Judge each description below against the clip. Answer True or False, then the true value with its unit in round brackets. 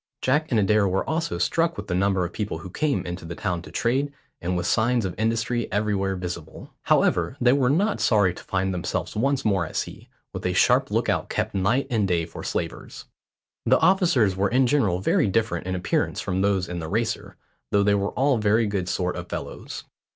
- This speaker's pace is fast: True (210 wpm)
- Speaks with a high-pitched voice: False (100 Hz)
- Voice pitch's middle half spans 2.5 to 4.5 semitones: False (5.1 semitones)